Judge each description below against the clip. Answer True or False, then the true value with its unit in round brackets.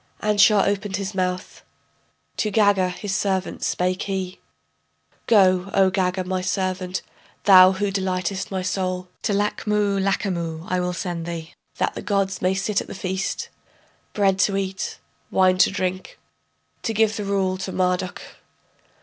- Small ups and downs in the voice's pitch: True (1.4 semitones)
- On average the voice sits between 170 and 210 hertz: True (190 Hz)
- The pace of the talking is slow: False (150 wpm)